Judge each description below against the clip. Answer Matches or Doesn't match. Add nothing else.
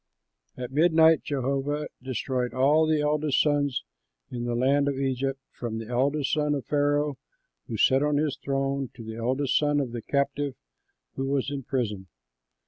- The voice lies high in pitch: Doesn't match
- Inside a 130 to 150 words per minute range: Doesn't match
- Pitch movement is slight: Matches